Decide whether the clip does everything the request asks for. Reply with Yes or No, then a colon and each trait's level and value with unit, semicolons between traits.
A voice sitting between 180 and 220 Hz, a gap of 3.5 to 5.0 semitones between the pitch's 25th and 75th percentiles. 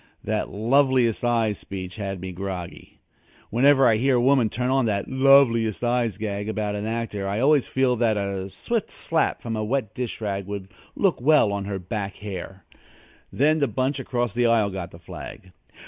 No: low, 110 Hz; average, 4.4 semitones